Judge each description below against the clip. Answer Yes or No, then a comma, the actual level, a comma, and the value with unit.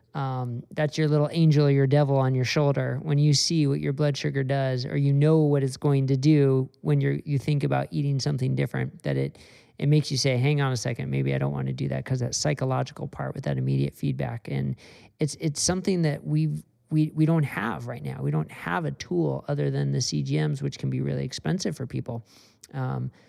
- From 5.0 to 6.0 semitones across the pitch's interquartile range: Yes, average, 5.3 semitones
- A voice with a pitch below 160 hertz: Yes, low, 135 Hz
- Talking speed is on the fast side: Yes, fast, 230 wpm